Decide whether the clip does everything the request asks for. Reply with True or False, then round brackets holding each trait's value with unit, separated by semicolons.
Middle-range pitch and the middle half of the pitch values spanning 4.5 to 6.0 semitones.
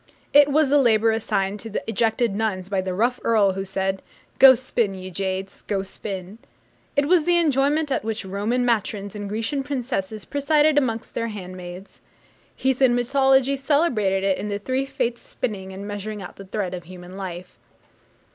False (220 Hz; 5.4 semitones)